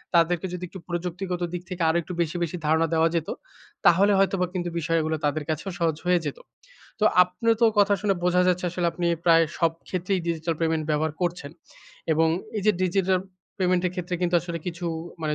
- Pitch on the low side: No, medium, 175 Hz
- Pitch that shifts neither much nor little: No, narrow, 1.8 semitones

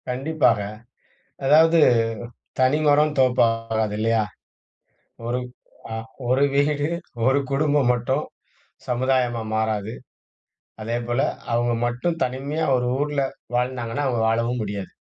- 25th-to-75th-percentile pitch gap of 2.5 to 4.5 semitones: Yes, average, 3.4 semitones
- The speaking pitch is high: No, low, 125 Hz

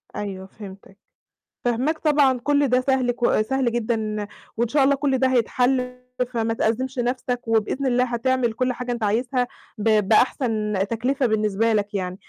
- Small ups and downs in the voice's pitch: No, average, 3.0 semitones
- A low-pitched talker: No, high, 240 Hz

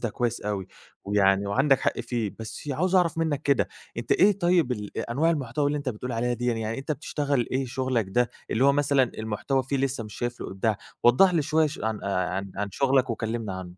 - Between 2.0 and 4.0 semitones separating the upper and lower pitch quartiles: No, average, 4.5 semitones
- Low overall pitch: Yes, low, 125 Hz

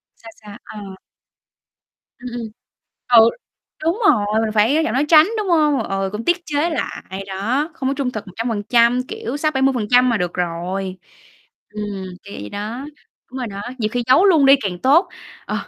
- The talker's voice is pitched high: Yes, high, 240 Hz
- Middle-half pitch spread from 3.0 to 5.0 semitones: No, wide, 5.5 semitones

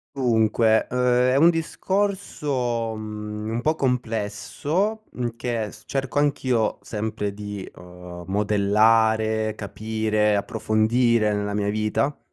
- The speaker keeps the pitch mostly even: No, average, 3.0 semitones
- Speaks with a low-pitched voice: Yes, low, 110 Hz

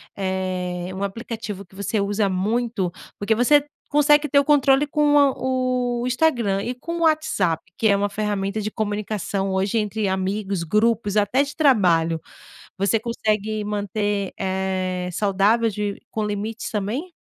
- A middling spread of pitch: Yes, average, 4.0 semitones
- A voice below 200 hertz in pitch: No, high, 210 Hz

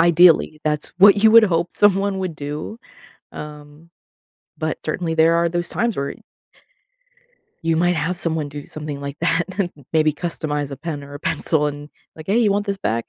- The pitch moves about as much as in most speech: Yes, average, 3.3 semitones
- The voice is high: No, medium, 160 Hz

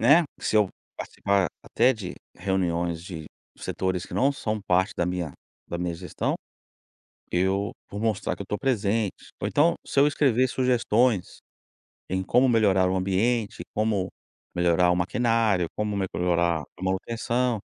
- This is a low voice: Yes, low, 100 Hz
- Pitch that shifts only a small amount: No, average, 4.3 semitones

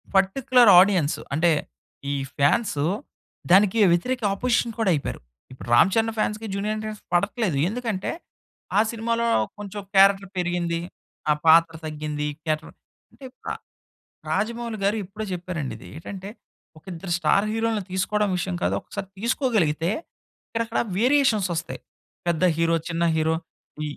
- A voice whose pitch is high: Yes, high, 195 Hz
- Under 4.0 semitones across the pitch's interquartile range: No, average, 4.9 semitones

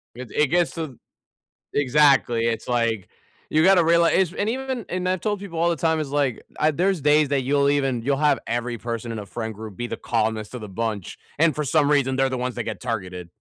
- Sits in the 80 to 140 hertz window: Yes, low, 135 Hz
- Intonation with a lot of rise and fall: Yes, wide, 5.7 semitones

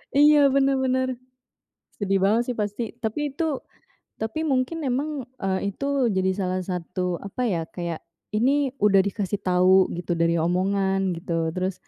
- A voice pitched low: No, high, 200 Hz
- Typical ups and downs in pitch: No, wide, 6.2 semitones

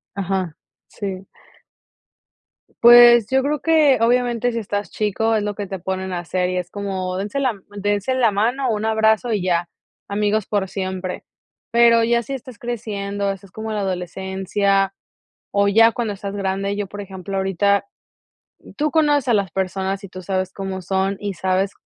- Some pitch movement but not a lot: Yes, average, 3.0 semitones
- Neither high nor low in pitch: No, high, 200 Hz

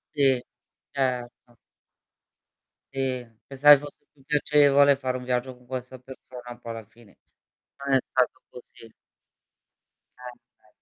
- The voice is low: Yes, low, 130 Hz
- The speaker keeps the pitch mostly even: Yes, narrow, 1.9 semitones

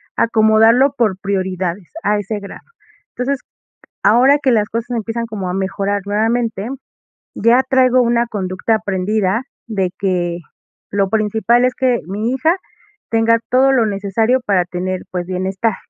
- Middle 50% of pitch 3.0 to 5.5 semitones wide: Yes, average, 3.6 semitones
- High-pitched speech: Yes, high, 215 Hz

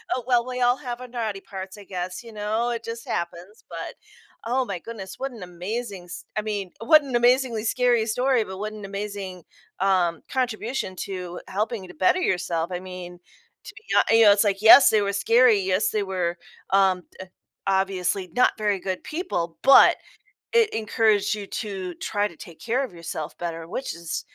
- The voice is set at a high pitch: Yes, high, 205 Hz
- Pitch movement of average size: Yes, average, 4.1 semitones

